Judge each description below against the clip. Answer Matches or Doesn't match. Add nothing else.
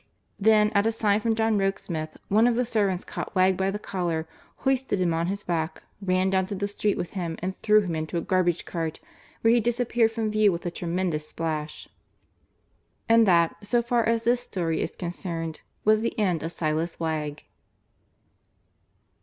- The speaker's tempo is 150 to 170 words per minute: Doesn't match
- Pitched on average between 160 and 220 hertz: Matches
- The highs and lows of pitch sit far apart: Doesn't match